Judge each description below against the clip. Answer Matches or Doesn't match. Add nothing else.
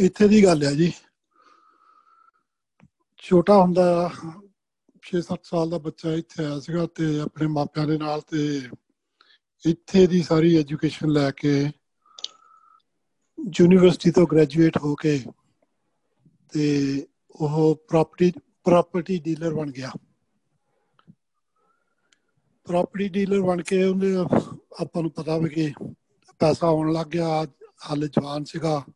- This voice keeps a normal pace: Matches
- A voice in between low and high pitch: Matches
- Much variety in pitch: Doesn't match